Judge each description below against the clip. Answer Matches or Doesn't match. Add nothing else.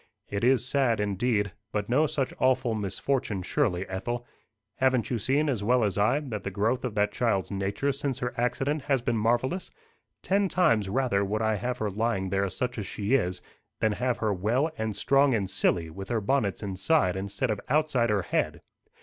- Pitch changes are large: Doesn't match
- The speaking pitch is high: Doesn't match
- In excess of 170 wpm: Matches